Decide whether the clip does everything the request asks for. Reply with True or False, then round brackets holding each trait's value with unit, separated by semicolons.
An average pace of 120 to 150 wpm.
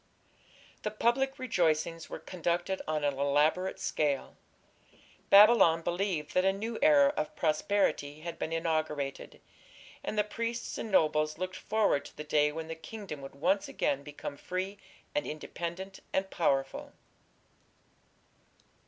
True (135 wpm)